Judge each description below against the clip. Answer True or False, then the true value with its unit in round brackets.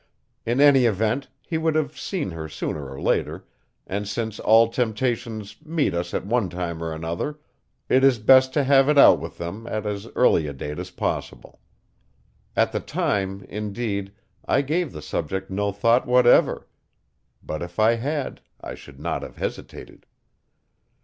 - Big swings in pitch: True (5.7 semitones)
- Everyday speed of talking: True (165 wpm)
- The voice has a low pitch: True (110 Hz)